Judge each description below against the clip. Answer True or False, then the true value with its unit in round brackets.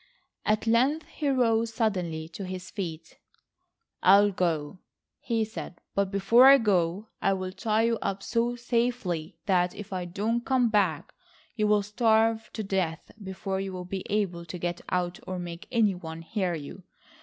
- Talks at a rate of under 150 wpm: False (155 wpm)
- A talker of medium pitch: False (195 Hz)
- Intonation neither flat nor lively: True (4.0 semitones)